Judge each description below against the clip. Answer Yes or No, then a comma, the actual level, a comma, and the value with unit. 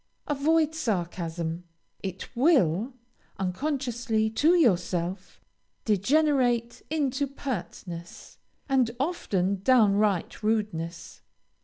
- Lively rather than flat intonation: Yes, wide, 7.2 semitones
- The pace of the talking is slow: Yes, slow, 70 wpm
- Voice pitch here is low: No, high, 220 Hz